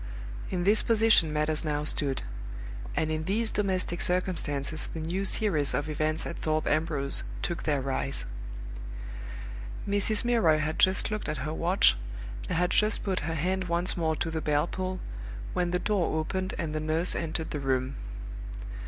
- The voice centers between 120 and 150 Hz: No, medium, 165 Hz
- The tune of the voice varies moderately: Yes, average, 3.5 semitones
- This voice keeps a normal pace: Yes, average, 165 wpm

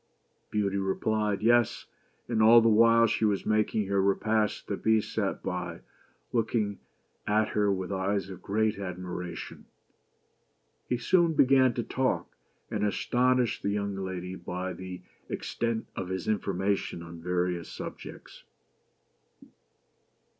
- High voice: No, low, 100 Hz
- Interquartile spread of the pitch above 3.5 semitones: No, average, 3.0 semitones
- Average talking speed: No, slow, 130 wpm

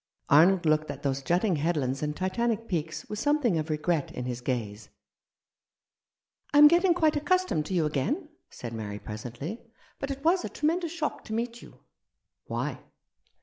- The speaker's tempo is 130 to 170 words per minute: No, average, 185 wpm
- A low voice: No, medium, 175 Hz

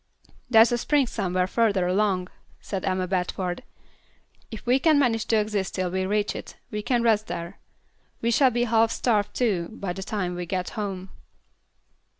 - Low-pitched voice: No, high, 205 Hz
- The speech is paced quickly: No, average, 170 wpm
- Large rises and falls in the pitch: No, average, 3.7 semitones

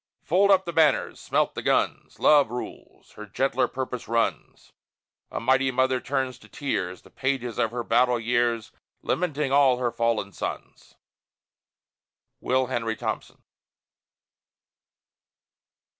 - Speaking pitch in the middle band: No, low, 125 Hz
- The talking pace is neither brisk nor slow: No, slow, 125 wpm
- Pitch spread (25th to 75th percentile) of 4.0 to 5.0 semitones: No, narrow, 2.6 semitones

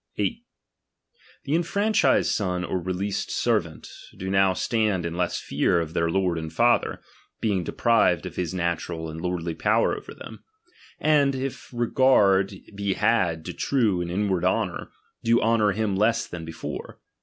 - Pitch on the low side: Yes, very low, 95 Hz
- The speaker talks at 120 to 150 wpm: No, average, 165 wpm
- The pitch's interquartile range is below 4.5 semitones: No, average, 4.8 semitones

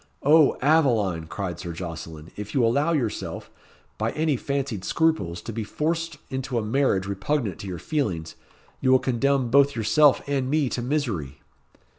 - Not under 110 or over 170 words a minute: Yes, average, 160 wpm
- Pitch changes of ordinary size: No, wide, 6.6 semitones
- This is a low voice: Yes, low, 125 Hz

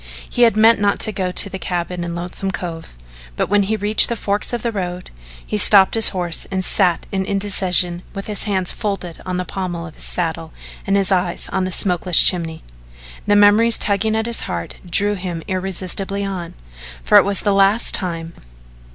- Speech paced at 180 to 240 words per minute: Yes, average, 195 wpm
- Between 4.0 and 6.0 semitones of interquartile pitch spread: No, narrow, 2.6 semitones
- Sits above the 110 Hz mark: Yes, high, 190 Hz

